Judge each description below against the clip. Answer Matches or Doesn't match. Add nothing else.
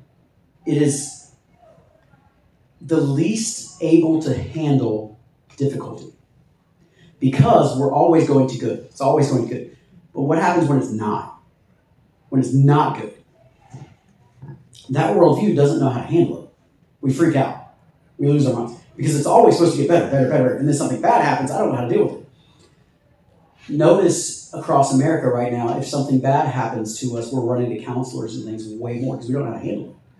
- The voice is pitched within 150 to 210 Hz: Doesn't match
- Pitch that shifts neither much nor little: Matches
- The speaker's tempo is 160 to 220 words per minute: Matches